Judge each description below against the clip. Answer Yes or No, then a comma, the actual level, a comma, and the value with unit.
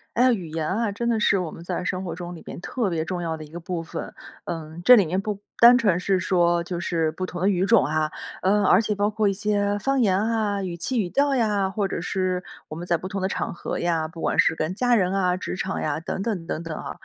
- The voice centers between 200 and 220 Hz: No, medium, 185 Hz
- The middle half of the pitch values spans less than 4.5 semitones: Yes, average, 3.4 semitones